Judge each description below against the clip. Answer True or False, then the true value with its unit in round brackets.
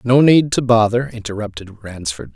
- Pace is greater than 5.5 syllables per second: False (4.9 syllables/s)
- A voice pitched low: True (115 Hz)